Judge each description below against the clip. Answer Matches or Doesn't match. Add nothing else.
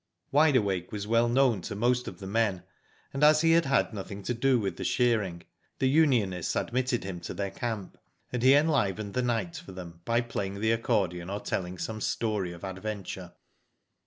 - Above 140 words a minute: Matches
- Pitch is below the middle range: Matches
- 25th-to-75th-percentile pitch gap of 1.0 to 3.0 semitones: Doesn't match